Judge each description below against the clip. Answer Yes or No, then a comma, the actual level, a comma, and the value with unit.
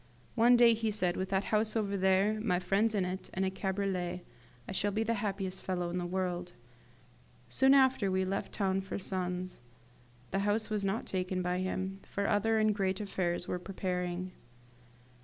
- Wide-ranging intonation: No, narrow, 2.4 semitones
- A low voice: No, high, 190 Hz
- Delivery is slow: No, average, 180 wpm